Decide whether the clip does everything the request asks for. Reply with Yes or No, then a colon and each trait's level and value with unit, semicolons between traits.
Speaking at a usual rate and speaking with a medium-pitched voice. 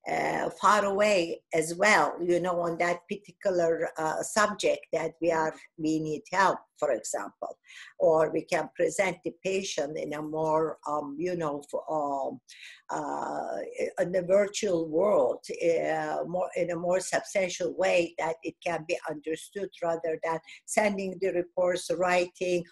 Yes: average, 150 wpm; medium, 175 Hz